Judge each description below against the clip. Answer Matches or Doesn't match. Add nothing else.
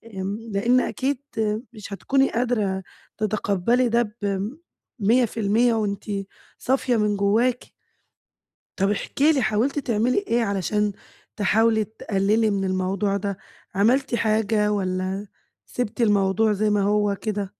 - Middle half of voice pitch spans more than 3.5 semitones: Doesn't match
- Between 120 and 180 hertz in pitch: Doesn't match